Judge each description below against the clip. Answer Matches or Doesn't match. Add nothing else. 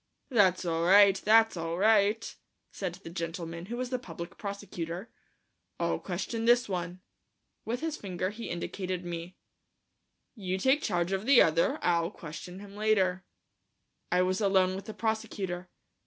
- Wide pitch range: Doesn't match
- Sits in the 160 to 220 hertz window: Matches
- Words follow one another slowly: Doesn't match